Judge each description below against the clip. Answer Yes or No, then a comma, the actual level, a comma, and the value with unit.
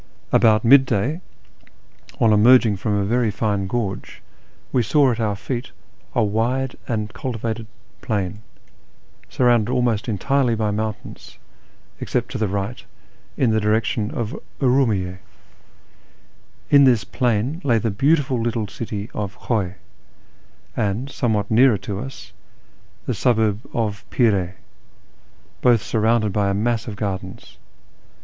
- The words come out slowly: Yes, slow, 130 wpm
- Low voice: Yes, low, 110 Hz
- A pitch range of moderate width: Yes, average, 3.1 semitones